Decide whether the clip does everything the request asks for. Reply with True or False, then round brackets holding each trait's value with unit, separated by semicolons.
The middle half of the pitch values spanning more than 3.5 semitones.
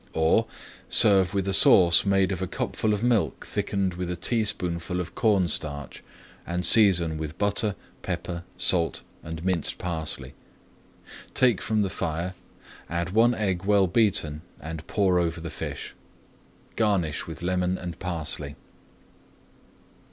False (3.2 semitones)